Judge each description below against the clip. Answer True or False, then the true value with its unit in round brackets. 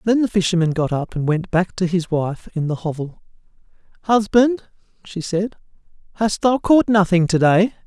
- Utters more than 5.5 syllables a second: False (4.9 syllables/s)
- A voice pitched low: False (190 Hz)